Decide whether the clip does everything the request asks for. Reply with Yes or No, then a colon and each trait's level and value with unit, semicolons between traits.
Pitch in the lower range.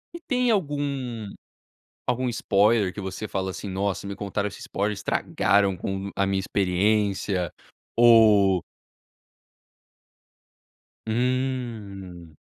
Yes: low, 100 Hz